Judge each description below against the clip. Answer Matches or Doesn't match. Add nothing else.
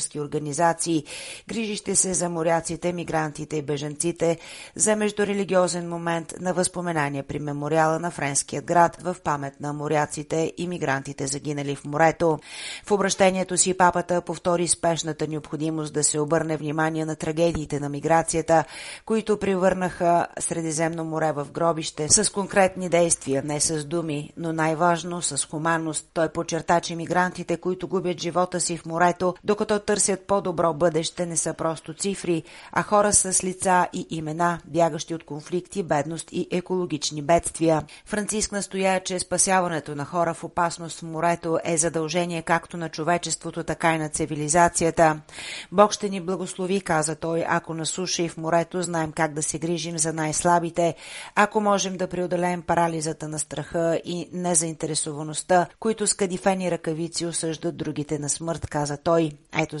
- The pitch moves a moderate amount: Doesn't match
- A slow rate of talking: Doesn't match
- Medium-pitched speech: Matches